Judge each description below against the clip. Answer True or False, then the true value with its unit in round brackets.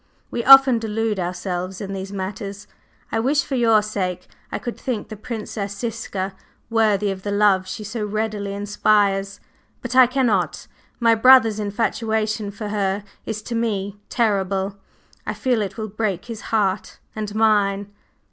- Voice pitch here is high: True (210 Hz)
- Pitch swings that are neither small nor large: False (2.3 semitones)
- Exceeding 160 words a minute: False (155 wpm)